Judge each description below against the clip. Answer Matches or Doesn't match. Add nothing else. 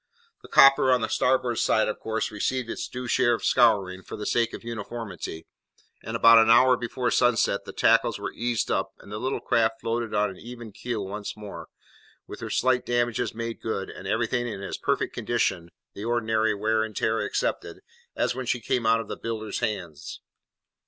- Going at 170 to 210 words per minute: Matches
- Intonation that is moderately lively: Doesn't match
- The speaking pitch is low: Matches